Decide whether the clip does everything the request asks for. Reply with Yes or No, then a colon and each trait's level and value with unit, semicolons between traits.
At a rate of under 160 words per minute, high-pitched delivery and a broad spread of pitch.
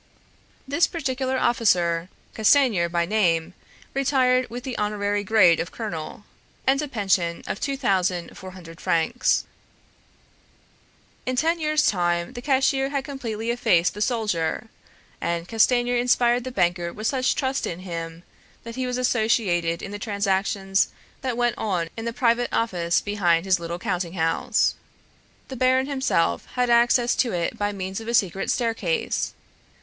Yes: average, 150 wpm; high, 220 Hz; wide, 6.1 semitones